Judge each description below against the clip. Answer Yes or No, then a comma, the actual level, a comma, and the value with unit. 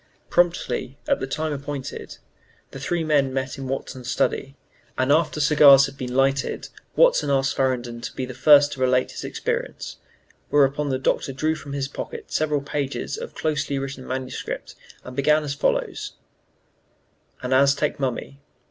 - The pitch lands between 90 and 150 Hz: Yes, medium, 140 Hz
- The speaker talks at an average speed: Yes, average, 155 wpm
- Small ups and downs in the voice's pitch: Yes, narrow, 2.0 semitones